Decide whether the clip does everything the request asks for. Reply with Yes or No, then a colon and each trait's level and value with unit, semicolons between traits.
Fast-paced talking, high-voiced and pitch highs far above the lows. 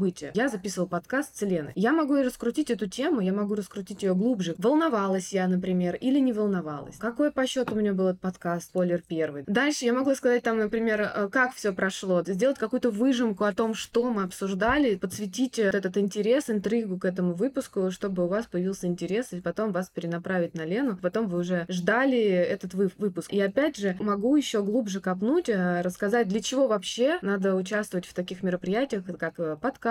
No: fast, 185 wpm; high, 205 Hz; average, 4.6 semitones